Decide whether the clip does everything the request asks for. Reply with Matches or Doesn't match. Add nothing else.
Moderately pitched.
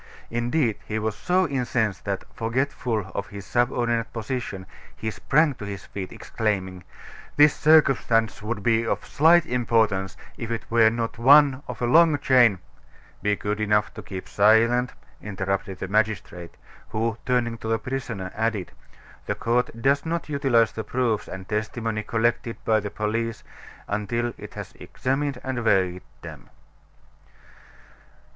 Doesn't match